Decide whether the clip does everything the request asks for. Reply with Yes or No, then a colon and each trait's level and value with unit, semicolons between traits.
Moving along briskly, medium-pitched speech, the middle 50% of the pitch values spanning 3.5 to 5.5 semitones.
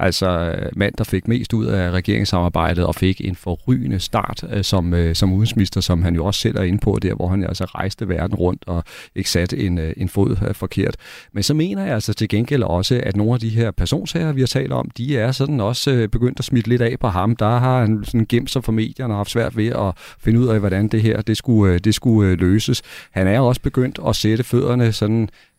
No: fast, 230 wpm; low, 110 Hz; average, 4.3 semitones